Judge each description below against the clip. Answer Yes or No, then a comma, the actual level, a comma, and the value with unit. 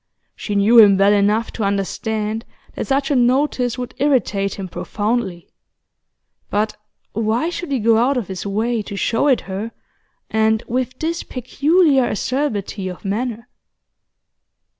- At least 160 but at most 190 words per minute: No, average, 140 wpm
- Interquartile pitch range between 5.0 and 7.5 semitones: No, average, 3.9 semitones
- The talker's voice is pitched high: Yes, high, 225 Hz